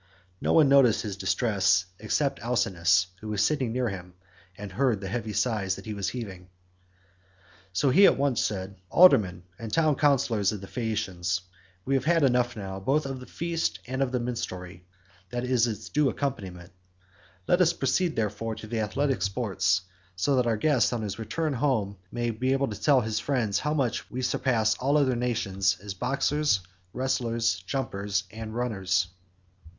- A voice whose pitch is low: Yes, low, 115 Hz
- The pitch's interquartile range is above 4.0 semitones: Yes, average, 5.1 semitones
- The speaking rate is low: No, average, 175 wpm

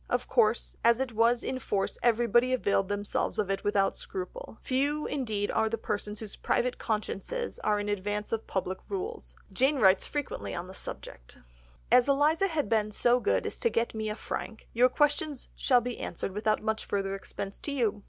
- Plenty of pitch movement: No, average, 4.0 semitones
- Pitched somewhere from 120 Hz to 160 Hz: No, high, 225 Hz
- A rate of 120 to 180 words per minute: No, average, 190 wpm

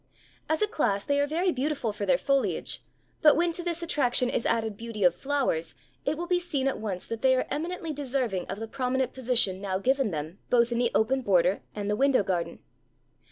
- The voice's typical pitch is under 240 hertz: No, very high, 255 Hz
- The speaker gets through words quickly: Yes, fast, 210 wpm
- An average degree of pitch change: No, wide, 5.7 semitones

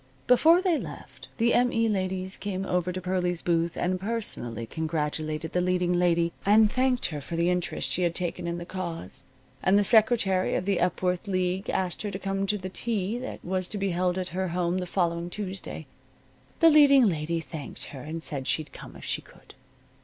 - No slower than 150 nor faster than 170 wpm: No, average, 200 wpm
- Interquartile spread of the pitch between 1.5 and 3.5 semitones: Yes, average, 2.9 semitones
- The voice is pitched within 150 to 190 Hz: Yes, medium, 185 Hz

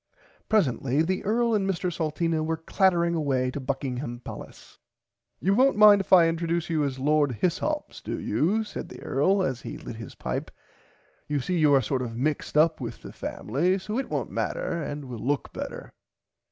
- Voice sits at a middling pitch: Yes, medium, 160 Hz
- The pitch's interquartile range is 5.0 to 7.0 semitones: Yes, wide, 5.4 semitones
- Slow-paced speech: No, average, 185 wpm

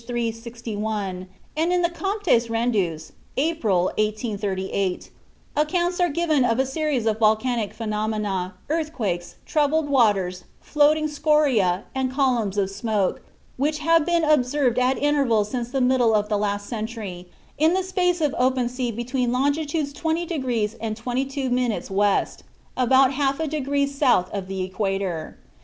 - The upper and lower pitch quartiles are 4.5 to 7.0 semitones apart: Yes, wide, 5.6 semitones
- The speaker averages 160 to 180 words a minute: No, average, 140 wpm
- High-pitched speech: Yes, very high, 250 Hz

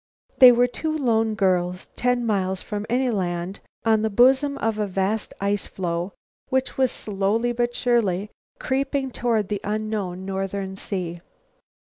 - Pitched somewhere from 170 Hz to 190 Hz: No, high, 215 Hz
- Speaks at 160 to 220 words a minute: No, average, 145 wpm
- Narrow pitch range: No, average, 4.1 semitones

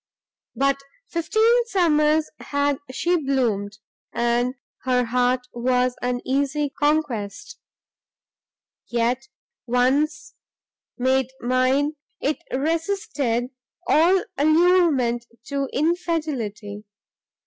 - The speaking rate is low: Yes, slow, 80 wpm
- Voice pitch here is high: Yes, very high, 275 Hz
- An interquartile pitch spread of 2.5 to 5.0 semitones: Yes, average, 4.0 semitones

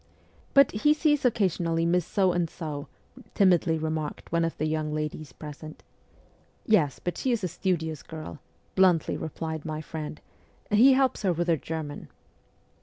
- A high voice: No, medium, 165 Hz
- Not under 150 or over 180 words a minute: Yes, average, 160 wpm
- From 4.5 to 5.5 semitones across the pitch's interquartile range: No, average, 3.5 semitones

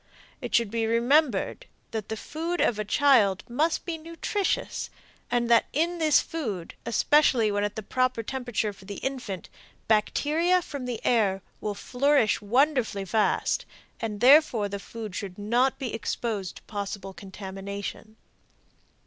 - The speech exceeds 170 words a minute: No, average, 145 wpm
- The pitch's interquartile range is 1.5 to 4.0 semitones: No, wide, 5.6 semitones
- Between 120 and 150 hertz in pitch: No, high, 230 Hz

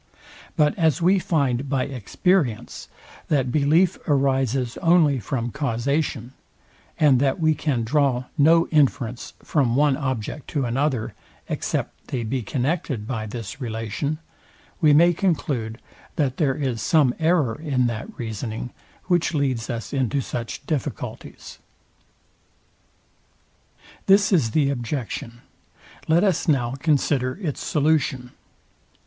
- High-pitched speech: No, low, 135 Hz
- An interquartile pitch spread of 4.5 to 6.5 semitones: No, average, 4.1 semitones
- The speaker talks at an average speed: No, slow, 120 wpm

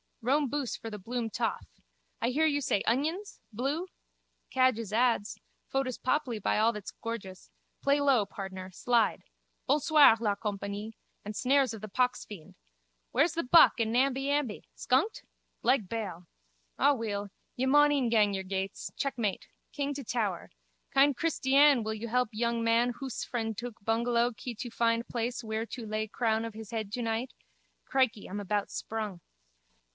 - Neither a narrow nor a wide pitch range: Yes, average, 3.8 semitones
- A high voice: Yes, high, 235 Hz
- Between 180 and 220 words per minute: No, average, 160 wpm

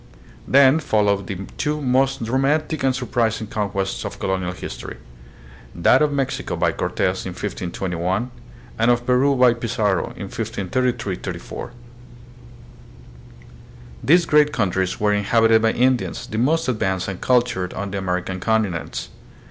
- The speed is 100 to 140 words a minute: Yes, slow, 135 wpm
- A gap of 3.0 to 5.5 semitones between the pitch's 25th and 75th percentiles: Yes, average, 5.1 semitones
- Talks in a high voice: No, low, 115 Hz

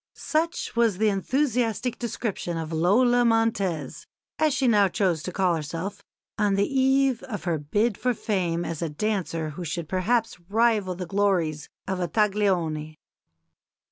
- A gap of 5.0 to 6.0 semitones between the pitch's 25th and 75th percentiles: Yes, average, 5.3 semitones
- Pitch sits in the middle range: No, high, 200 Hz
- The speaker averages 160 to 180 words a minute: No, average, 150 wpm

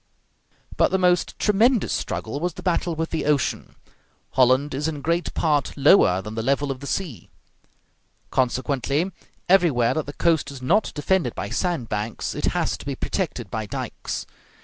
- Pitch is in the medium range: Yes, medium, 145 Hz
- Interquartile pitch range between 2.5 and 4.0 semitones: No, average, 5.2 semitones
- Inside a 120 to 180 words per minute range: Yes, average, 170 wpm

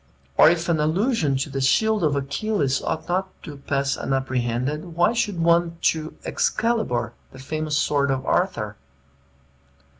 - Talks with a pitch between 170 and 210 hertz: No, medium, 155 Hz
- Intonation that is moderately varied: Yes, average, 4.3 semitones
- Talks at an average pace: Yes, average, 145 wpm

